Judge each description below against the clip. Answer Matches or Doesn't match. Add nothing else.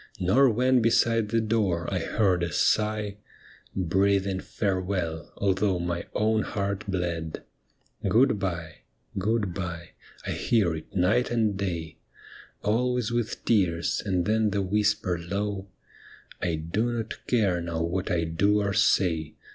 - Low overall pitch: Matches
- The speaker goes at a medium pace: Matches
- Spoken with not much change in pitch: Doesn't match